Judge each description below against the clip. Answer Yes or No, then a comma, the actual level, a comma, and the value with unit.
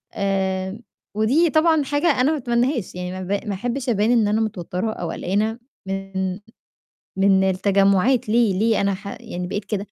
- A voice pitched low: No, high, 205 Hz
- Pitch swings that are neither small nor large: Yes, average, 3.8 semitones